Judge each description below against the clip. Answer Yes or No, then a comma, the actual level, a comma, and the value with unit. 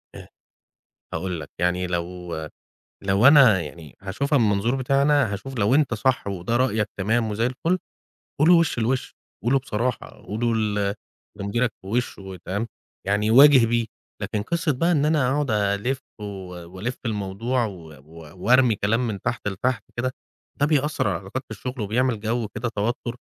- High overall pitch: No, low, 110 Hz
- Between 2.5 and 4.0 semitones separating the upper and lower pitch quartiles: No, average, 4.5 semitones